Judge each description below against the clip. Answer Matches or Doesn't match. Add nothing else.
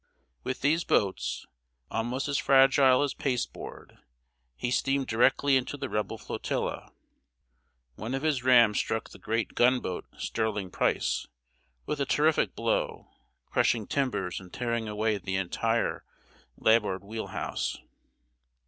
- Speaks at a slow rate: Matches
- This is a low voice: Matches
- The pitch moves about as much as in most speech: Matches